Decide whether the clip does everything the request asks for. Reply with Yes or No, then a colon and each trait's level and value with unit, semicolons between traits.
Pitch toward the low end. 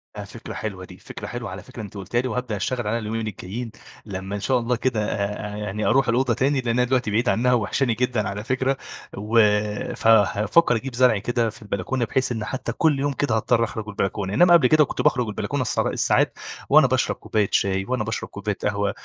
Yes: low, 115 Hz